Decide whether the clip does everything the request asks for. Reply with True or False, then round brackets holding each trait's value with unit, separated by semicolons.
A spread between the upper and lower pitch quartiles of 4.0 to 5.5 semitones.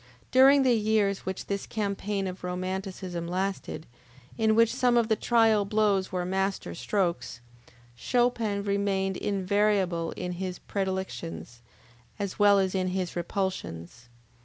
False (2.5 semitones)